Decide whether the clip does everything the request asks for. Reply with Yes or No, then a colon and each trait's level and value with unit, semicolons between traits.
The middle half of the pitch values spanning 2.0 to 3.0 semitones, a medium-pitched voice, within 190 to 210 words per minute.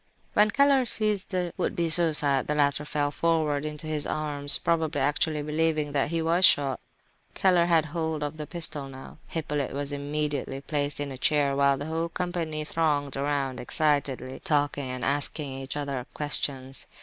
No: narrow, 2.4 semitones; medium, 150 Hz; average, 170 wpm